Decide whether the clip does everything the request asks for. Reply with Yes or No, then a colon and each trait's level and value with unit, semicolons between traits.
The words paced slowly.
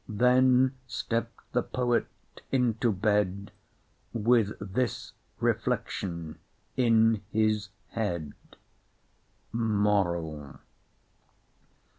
Yes: slow, 65 wpm